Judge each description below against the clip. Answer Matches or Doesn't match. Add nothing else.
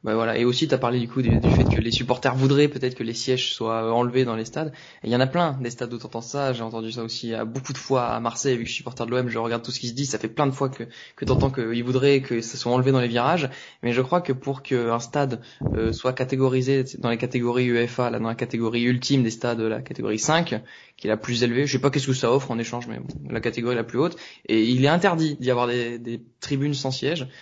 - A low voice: Matches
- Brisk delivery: Matches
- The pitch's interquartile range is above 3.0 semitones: Doesn't match